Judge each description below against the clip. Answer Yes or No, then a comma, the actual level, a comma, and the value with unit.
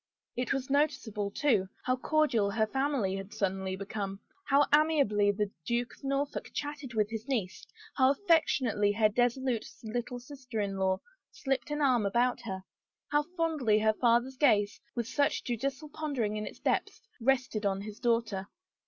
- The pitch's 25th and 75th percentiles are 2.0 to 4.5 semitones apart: No, average, 4.9 semitones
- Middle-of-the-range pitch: No, high, 240 Hz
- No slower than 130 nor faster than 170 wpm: Yes, average, 160 wpm